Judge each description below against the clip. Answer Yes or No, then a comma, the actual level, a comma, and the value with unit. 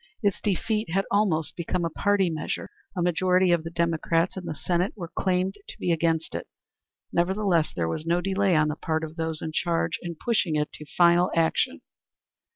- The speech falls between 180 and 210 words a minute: Yes, average, 190 wpm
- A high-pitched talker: No, medium, 170 Hz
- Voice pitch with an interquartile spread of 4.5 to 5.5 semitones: No, narrow, 2.5 semitones